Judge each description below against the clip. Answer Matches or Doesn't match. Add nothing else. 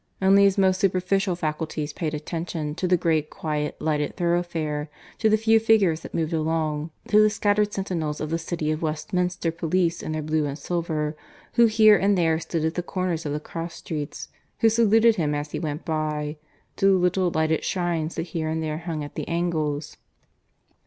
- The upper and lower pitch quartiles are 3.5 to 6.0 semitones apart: Doesn't match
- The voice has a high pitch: Doesn't match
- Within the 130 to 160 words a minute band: Doesn't match